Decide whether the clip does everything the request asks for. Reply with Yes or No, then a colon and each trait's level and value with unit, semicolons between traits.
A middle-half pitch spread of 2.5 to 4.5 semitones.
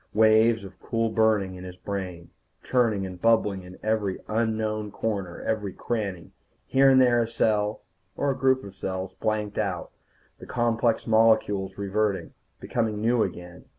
Yes: average, 2.9 semitones